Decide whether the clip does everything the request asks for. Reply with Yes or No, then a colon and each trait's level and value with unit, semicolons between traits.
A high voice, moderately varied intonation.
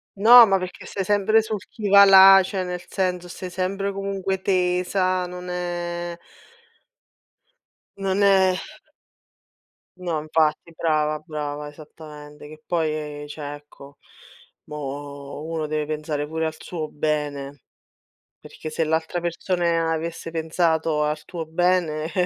No: medium, 165 Hz; average, 3.2 semitones